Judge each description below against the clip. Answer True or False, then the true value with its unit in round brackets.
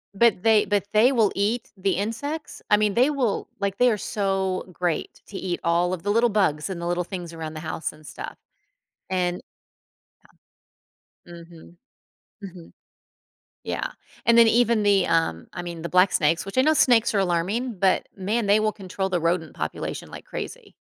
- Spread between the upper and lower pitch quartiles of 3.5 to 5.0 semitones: True (4.1 semitones)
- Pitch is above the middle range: True (195 Hz)